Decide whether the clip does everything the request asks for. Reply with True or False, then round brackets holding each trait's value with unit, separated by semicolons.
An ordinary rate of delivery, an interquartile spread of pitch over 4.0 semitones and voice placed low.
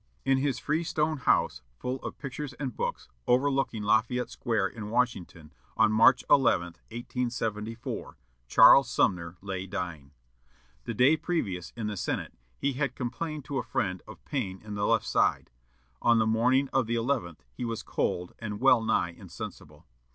True (160 wpm; 4.5 semitones; 115 Hz)